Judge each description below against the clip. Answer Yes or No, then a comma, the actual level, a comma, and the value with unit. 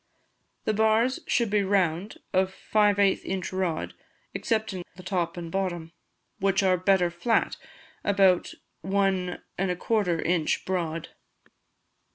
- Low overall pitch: No, high, 190 Hz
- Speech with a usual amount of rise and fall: No, narrow, 2.3 semitones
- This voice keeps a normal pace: No, slow, 120 wpm